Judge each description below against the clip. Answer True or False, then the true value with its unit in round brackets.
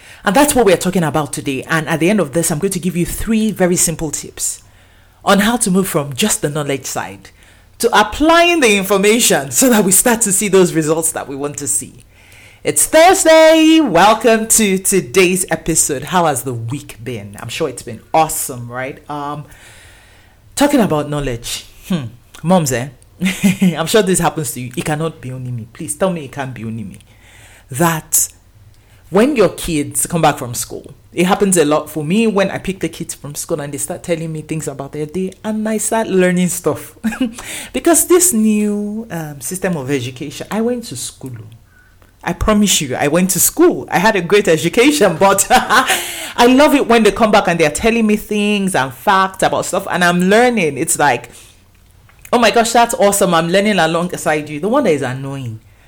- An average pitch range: False (7.5 semitones)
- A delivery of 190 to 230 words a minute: True (200 wpm)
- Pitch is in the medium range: True (165 Hz)